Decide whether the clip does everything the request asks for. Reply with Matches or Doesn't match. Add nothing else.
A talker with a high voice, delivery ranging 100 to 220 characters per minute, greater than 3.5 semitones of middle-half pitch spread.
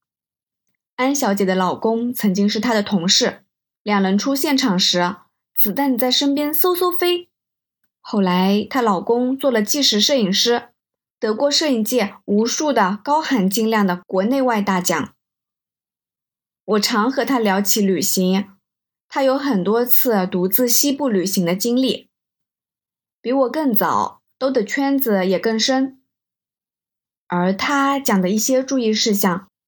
Matches